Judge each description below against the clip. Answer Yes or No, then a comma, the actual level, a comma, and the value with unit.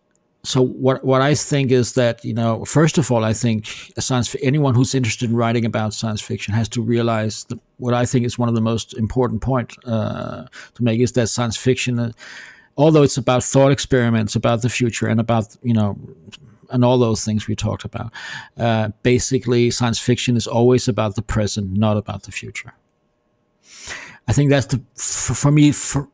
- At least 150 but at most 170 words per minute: No, average, 200 wpm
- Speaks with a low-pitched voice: Yes, low, 120 Hz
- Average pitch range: No, narrow, 2.3 semitones